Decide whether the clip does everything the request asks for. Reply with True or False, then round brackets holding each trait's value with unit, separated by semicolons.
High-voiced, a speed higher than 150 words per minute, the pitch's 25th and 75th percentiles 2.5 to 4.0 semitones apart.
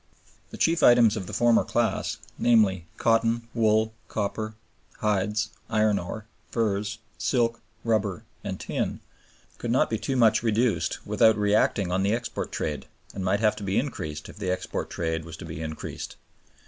False (105 Hz; 160 wpm; 3.2 semitones)